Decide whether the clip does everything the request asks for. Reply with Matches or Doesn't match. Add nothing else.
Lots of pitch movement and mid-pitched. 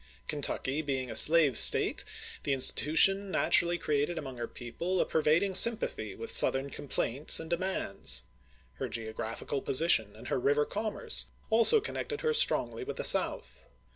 Matches